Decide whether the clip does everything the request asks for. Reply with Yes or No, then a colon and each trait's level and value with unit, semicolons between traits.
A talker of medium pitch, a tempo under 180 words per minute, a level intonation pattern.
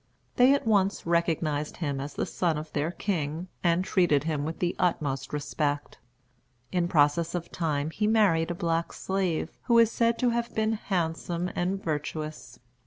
No: medium, 170 Hz; average, 170 wpm; average, 3.9 semitones